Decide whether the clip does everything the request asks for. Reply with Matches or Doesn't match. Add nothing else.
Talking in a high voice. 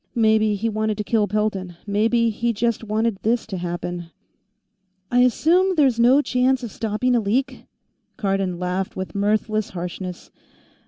Matches